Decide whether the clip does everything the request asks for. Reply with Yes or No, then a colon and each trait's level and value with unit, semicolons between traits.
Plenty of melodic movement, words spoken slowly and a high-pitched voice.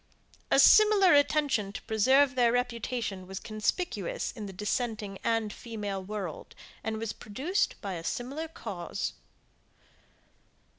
No: average, 5.0 semitones; slow, 120 wpm; high, 225 Hz